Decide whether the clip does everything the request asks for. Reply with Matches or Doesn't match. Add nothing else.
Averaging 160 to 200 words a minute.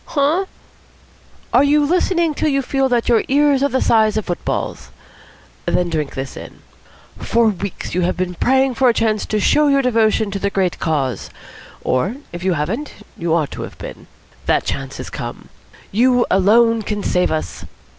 Matches